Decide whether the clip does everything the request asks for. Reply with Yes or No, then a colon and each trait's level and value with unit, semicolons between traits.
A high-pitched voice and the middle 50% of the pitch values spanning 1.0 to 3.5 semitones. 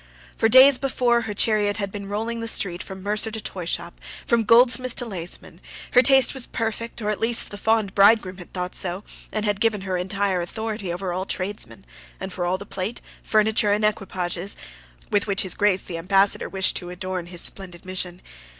Yes: high, 200 Hz; average, 3.2 semitones